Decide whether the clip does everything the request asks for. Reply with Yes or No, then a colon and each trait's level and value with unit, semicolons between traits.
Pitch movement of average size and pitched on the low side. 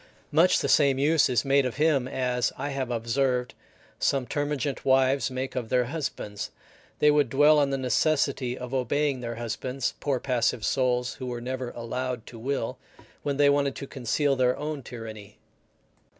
No: narrow, 2.3 semitones; low, 130 Hz